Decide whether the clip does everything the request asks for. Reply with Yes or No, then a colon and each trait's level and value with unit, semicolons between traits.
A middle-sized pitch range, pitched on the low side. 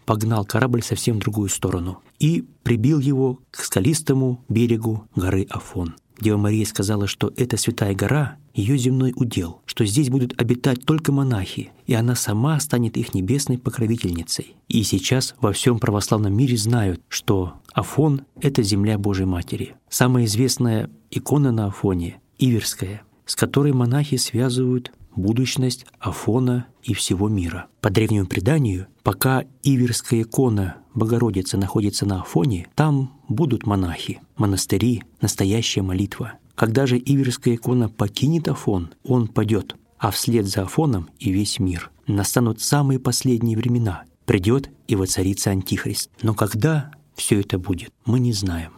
Yes: average, 4.3 semitones; low, 115 Hz